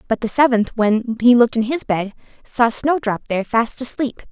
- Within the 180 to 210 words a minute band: Yes, average, 195 wpm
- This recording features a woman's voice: Yes, female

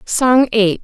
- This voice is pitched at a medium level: No, high, 225 Hz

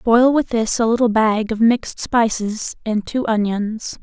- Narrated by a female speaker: Yes, female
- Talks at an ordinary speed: Yes, average, 180 wpm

